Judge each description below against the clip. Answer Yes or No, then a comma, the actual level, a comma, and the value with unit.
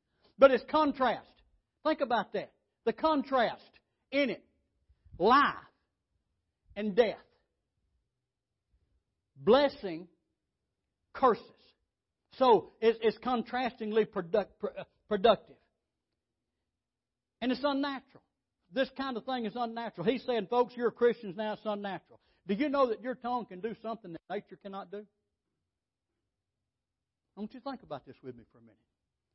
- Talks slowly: Yes, slow, 125 wpm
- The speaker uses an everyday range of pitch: No, wide, 6.9 semitones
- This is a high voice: Yes, high, 220 Hz